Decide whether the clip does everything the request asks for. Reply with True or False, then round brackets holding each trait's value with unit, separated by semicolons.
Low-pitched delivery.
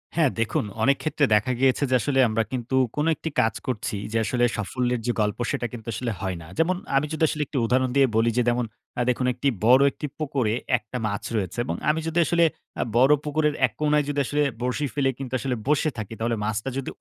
True (130 Hz)